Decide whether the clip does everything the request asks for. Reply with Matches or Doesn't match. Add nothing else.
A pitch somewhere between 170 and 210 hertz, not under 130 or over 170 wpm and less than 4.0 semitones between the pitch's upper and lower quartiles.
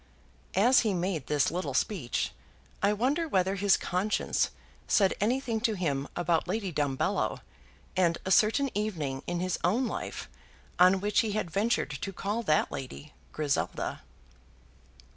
Doesn't match